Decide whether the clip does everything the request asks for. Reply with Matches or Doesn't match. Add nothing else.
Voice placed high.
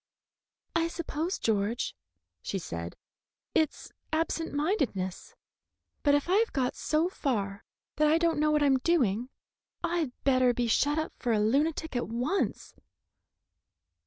Matches